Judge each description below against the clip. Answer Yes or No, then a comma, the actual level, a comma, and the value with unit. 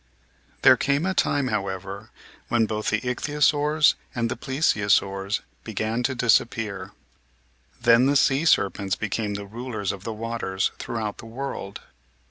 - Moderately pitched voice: No, low, 115 Hz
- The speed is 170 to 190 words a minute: No, average, 140 wpm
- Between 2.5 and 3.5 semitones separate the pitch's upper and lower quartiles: No, average, 4.5 semitones